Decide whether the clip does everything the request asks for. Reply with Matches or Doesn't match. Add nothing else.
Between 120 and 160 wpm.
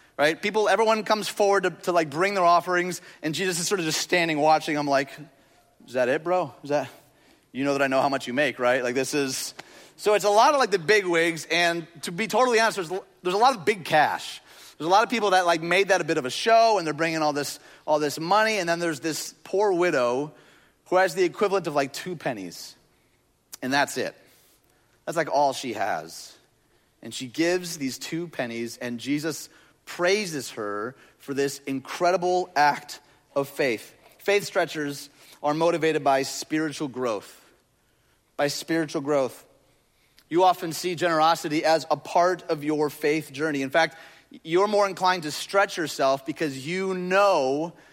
Doesn't match